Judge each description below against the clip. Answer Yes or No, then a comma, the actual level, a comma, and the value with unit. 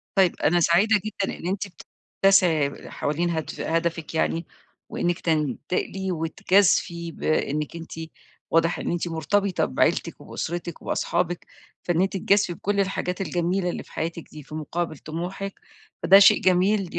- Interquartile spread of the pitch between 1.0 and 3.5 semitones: Yes, average, 2.8 semitones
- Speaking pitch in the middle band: Yes, medium, 175 Hz